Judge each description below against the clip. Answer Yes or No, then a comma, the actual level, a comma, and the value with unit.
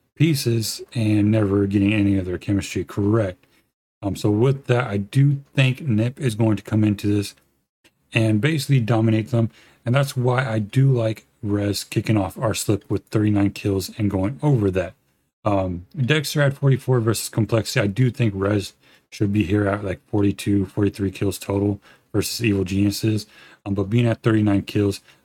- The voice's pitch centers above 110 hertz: No, low, 105 Hz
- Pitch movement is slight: No, average, 3.5 semitones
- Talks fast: No, average, 175 wpm